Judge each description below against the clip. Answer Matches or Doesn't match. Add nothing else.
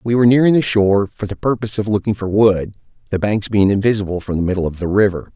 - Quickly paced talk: Matches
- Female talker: Doesn't match